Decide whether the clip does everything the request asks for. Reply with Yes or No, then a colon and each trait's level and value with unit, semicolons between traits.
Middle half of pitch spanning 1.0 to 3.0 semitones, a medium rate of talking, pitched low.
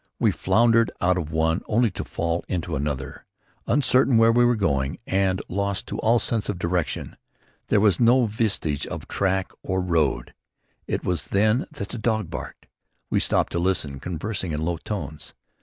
No: average, 4.9 semitones; average, 175 wpm; very low, 95 Hz